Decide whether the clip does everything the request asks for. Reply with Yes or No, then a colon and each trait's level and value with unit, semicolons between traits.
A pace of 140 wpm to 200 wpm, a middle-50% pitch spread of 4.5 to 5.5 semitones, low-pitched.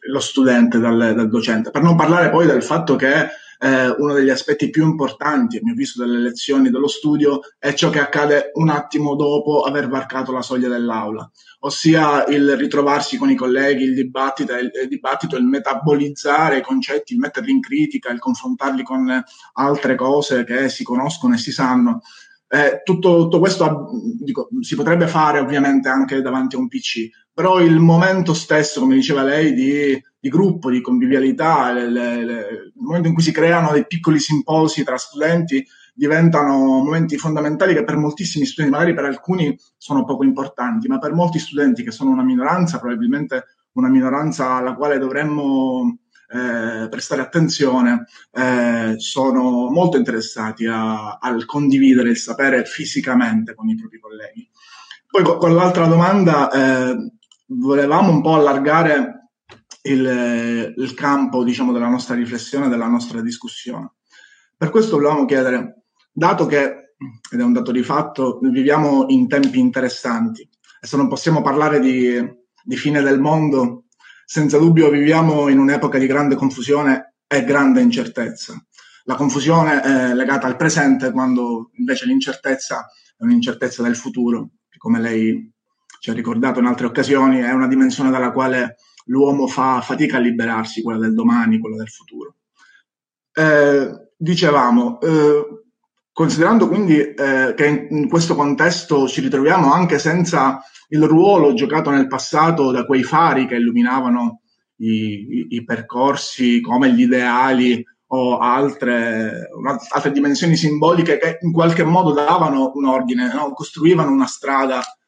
No: average, 150 wpm; average, 5.0 semitones; medium, 145 Hz